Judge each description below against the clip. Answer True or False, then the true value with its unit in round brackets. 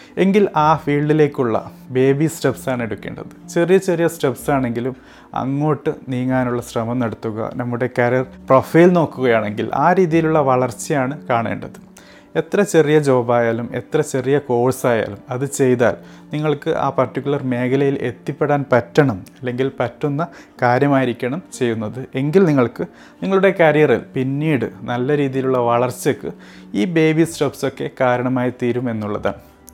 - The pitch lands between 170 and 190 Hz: False (135 Hz)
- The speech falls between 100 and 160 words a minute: True (105 wpm)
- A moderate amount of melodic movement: True (3.8 semitones)